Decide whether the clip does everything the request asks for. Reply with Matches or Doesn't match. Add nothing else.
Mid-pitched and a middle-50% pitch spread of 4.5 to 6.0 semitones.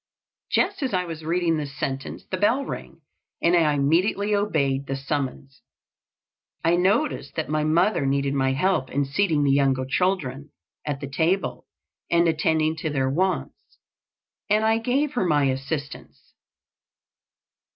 Matches